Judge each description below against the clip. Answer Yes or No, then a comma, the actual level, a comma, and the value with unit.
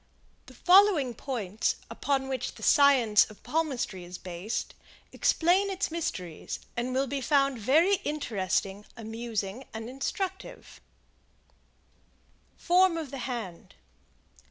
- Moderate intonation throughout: No, wide, 6.9 semitones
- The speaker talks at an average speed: No, slow, 115 wpm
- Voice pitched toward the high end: Yes, very high, 260 Hz